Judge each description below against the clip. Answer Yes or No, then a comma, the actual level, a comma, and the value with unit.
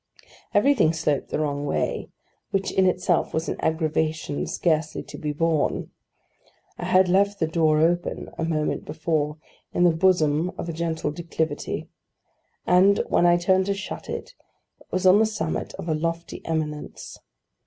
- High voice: No, medium, 165 Hz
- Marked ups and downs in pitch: No, average, 2.7 semitones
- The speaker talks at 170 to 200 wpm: No, average, 160 wpm